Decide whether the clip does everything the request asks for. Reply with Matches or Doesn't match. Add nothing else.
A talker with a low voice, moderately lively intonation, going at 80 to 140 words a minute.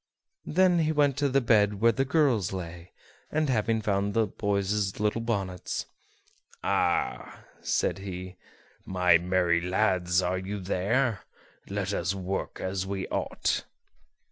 Matches